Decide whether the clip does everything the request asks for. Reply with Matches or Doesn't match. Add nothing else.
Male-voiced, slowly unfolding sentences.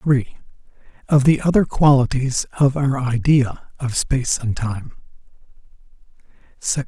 Matches